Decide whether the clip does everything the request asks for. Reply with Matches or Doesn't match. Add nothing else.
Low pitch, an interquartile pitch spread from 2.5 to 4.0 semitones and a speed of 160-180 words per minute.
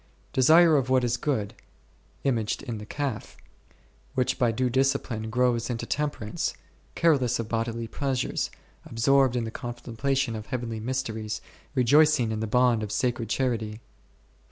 Doesn't match